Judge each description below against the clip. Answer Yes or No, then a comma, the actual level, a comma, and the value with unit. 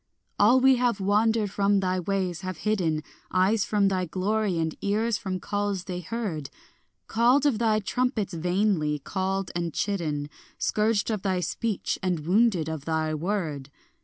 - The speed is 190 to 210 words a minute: No, average, 155 wpm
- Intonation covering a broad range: No, average, 3.6 semitones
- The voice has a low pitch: No, high, 195 Hz